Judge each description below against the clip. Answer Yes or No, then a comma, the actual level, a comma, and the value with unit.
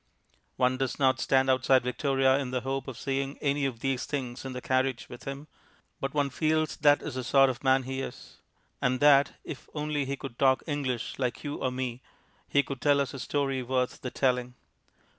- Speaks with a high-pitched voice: No, low, 135 Hz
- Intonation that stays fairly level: Yes, narrow, 1.5 semitones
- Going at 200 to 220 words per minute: Yes, fast, 205 wpm